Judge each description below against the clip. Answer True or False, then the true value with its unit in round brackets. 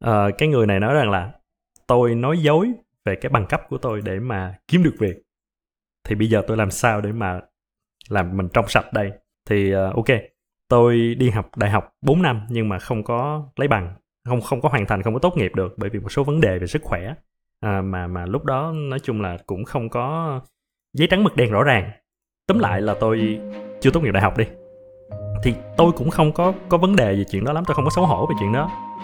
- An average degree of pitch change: False (6.5 semitones)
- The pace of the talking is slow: False (240 wpm)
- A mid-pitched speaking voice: False (115 Hz)